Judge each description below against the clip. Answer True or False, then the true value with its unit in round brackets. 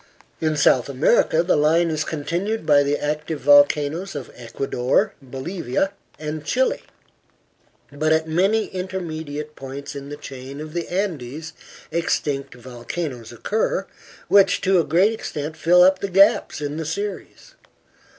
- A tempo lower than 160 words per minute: True (140 wpm)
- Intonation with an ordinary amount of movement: True (4.1 semitones)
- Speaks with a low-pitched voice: False (155 Hz)